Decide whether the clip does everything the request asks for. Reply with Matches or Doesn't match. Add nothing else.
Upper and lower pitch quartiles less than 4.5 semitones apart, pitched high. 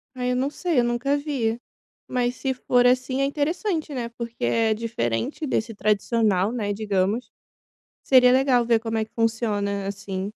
Matches